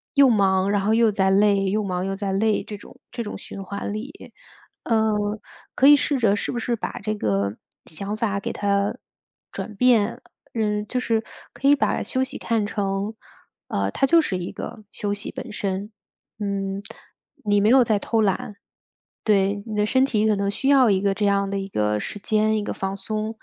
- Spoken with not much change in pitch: Yes, narrow, 2.2 semitones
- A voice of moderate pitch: No, high, 205 Hz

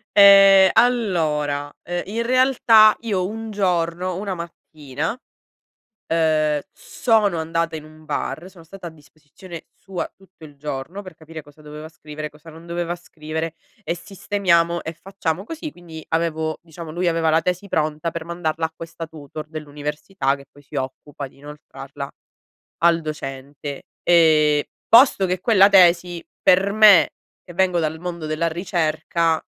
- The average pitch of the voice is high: No, medium, 165 Hz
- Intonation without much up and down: No, average, 3.2 semitones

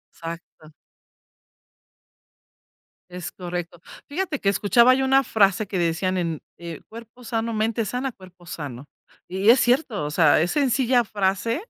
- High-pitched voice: Yes, high, 200 Hz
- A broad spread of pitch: Yes, wide, 5.8 semitones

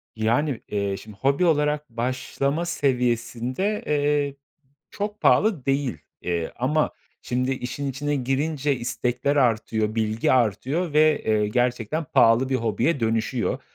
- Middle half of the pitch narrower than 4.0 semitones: No, average, 4.3 semitones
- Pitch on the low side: Yes, low, 130 Hz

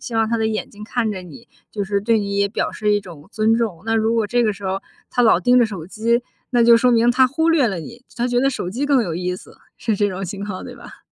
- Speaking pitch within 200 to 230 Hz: Yes, high, 220 Hz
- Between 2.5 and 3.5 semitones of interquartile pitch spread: Yes, average, 3.1 semitones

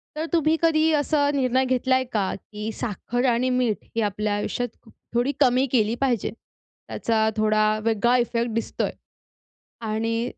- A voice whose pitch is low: No, high, 240 Hz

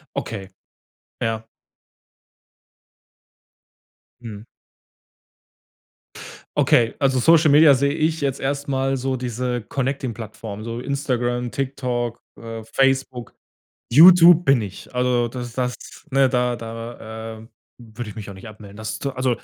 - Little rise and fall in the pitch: No, average, 3.0 semitones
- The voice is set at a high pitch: No, low, 125 Hz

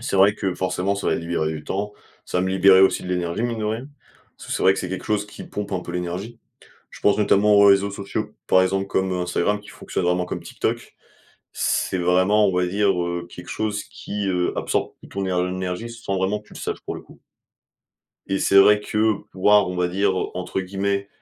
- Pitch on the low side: Yes, very low, 95 Hz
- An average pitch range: No, narrow, 2.3 semitones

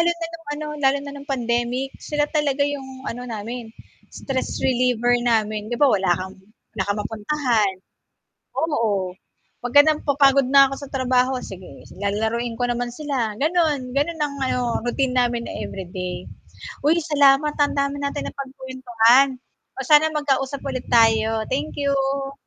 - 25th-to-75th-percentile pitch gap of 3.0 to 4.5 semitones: Yes, average, 3.5 semitones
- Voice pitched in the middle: No, very high, 260 Hz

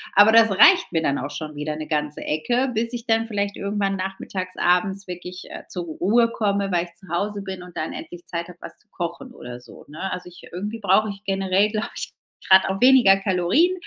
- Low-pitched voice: No, high, 195 Hz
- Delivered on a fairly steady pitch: No, average, 3.5 semitones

